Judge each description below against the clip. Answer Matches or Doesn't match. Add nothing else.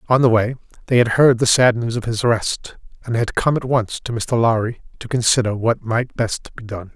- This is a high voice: Doesn't match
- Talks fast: Matches